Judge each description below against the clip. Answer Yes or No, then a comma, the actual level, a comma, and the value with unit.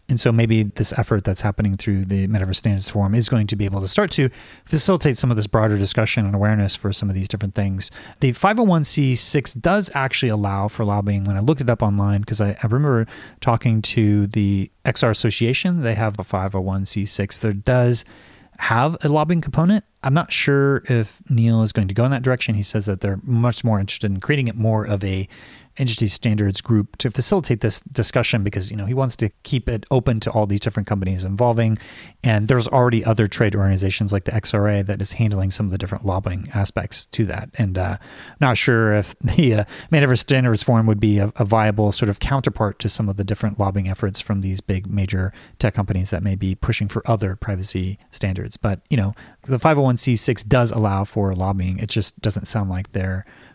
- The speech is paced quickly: Yes, fast, 210 wpm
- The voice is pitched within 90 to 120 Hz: Yes, low, 110 Hz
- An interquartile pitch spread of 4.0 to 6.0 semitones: No, average, 3.5 semitones